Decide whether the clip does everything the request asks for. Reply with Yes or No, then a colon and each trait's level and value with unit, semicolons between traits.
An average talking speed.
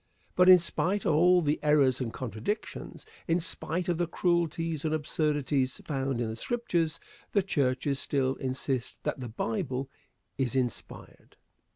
Yes: average, 150 wpm